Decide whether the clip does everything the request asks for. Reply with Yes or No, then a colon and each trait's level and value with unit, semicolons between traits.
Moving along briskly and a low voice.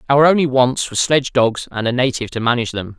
Yes: fast, 240 wpm; low, 125 Hz